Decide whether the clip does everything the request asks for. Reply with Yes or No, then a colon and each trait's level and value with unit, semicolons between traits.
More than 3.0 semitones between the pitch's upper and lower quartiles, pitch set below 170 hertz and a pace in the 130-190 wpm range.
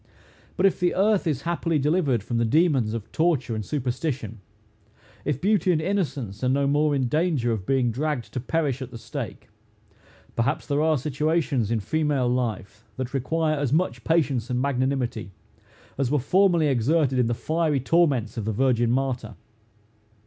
Yes: average, 4.7 semitones; low, 135 Hz; average, 170 wpm